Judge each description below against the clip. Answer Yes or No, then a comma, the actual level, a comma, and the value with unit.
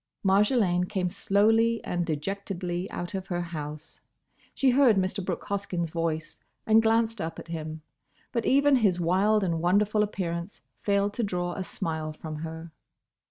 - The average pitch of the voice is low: No, medium, 185 Hz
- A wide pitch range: No, average, 3.8 semitones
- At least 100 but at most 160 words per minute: Yes, average, 155 wpm